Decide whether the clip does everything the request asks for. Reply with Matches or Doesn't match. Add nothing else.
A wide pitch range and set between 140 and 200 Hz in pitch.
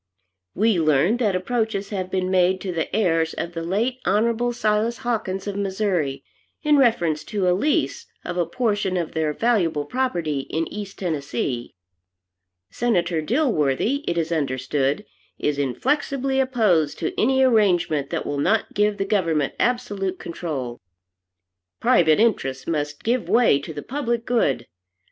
Matches